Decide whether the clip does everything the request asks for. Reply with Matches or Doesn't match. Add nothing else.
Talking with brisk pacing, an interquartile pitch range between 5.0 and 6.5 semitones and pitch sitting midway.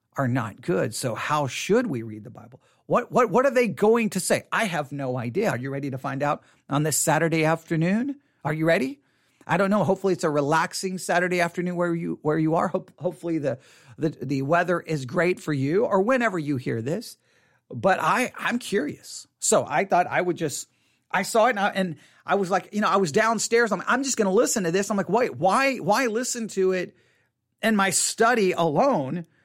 Matches